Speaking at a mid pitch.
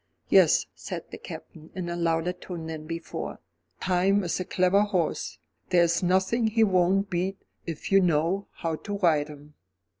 Yes: medium, 180 Hz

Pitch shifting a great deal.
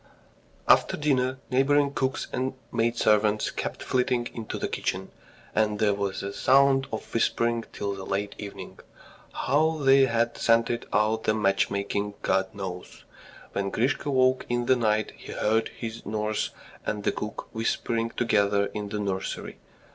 No: average, 3.8 semitones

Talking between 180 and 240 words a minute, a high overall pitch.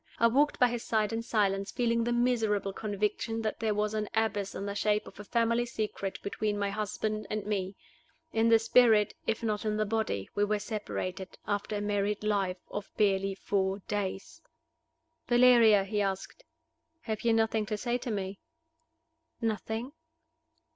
No: average, 170 wpm; high, 210 Hz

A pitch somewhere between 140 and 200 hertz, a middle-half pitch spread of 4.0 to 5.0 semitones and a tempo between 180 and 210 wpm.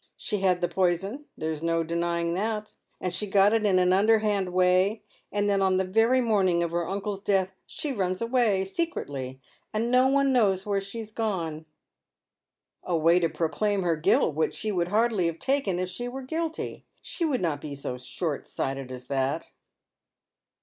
Yes: high, 190 Hz; average, 4.4 semitones; average, 190 wpm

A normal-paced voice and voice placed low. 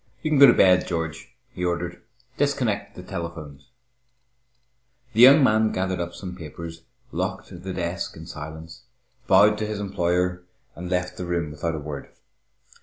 Yes: average, 160 wpm; very low, 90 Hz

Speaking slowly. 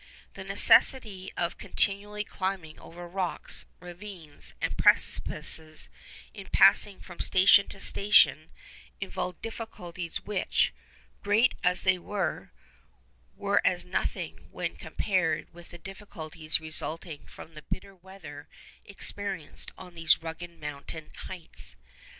Yes: slow, 115 wpm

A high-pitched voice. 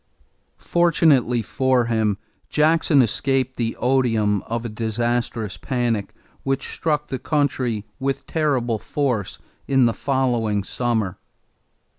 No: low, 120 Hz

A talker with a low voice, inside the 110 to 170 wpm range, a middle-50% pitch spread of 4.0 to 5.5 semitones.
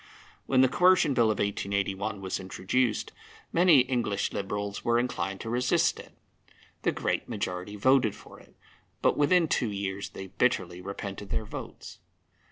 Yes: low, 105 Hz; average, 150 wpm; average, 4.3 semitones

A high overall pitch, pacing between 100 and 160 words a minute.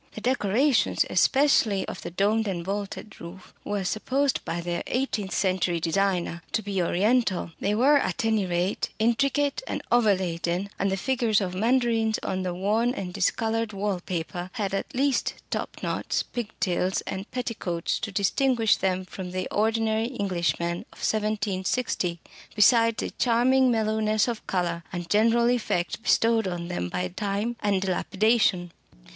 Yes: high, 205 Hz; average, 150 wpm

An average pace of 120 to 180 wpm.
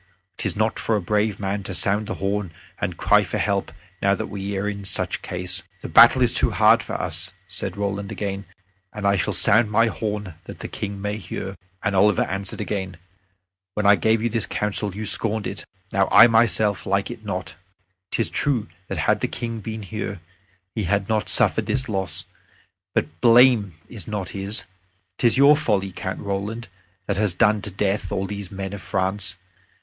No: average, 195 wpm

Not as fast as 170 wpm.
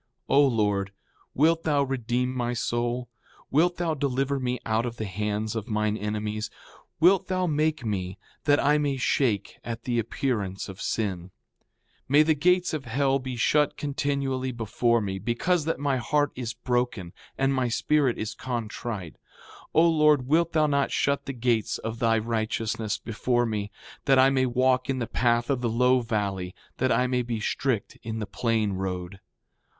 No: average, 175 wpm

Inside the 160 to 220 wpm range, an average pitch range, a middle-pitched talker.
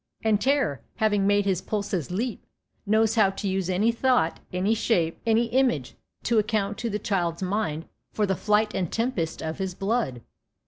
No: average, 175 wpm; average, 3.3 semitones; high, 205 Hz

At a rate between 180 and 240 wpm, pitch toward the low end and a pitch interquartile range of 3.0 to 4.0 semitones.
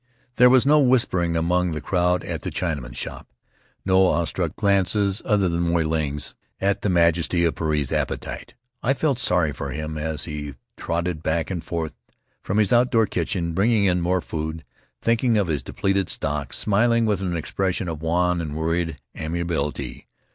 No: average, 170 wpm; very low, 85 Hz; average, 3.7 semitones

